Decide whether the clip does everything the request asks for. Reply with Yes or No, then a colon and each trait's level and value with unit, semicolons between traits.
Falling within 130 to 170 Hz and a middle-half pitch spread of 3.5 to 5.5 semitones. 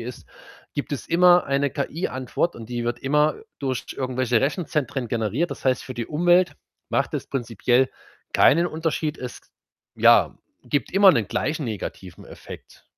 Yes: low, 135 Hz; average, 4.5 semitones